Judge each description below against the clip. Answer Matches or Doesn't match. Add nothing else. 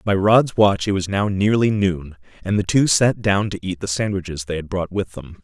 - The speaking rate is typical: Doesn't match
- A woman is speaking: Doesn't match